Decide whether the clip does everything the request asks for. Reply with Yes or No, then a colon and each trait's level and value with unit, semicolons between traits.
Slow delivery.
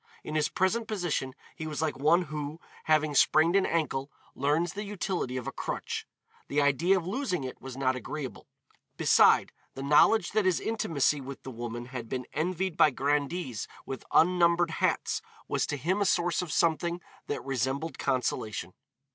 No: average, 170 wpm